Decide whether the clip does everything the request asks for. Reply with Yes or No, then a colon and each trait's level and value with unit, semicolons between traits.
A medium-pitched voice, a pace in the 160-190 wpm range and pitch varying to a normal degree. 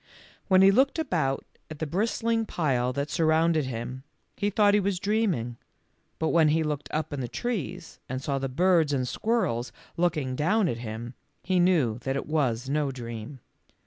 No: medium, 150 Hz; average, 180 wpm; wide, 6.3 semitones